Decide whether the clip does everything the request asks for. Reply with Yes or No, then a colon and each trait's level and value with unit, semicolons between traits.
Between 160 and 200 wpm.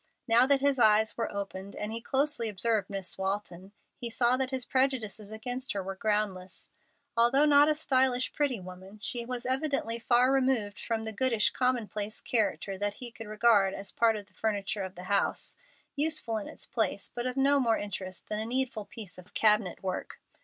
Yes: average, 190 wpm